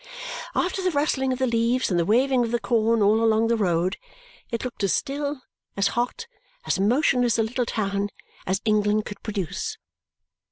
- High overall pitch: Yes, high, 230 Hz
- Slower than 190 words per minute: Yes, average, 175 wpm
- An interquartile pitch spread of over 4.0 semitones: No, average, 3.6 semitones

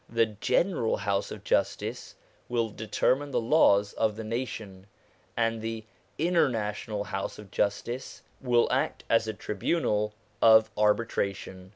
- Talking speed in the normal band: No, slow, 130 wpm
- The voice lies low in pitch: Yes, low, 110 Hz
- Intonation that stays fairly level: Yes, narrow, 2.1 semitones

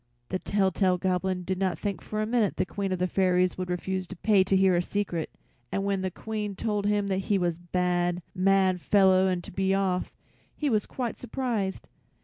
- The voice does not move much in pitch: Yes, narrow, 1.9 semitones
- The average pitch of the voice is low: No, high, 190 Hz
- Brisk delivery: Yes, fast, 210 wpm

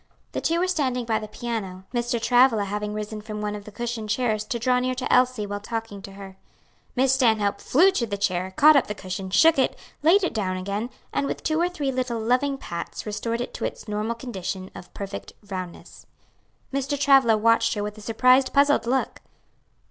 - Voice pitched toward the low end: No, high, 230 Hz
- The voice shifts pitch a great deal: No, average, 3.8 semitones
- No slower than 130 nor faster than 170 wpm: No, fast, 205 wpm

